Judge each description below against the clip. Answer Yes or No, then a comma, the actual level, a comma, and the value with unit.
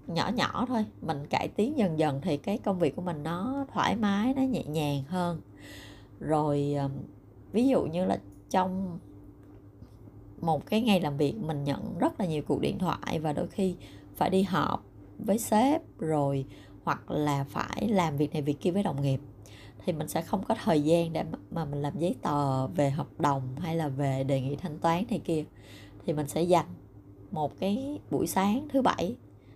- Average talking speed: Yes, average, 195 wpm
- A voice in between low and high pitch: Yes, medium, 155 Hz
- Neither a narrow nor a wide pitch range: No, wide, 5.9 semitones